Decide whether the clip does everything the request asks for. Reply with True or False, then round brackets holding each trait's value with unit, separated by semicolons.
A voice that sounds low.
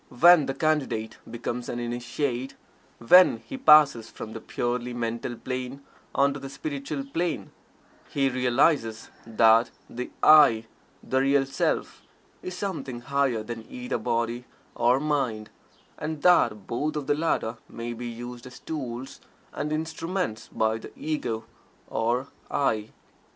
True (125 Hz)